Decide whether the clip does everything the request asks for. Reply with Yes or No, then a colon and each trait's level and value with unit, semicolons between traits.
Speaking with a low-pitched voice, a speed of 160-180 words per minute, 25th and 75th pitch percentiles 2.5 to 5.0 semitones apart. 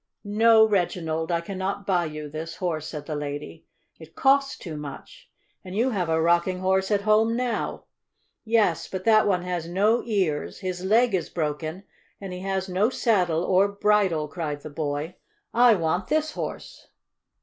No: medium, 185 Hz; average, 170 wpm; average, 4.4 semitones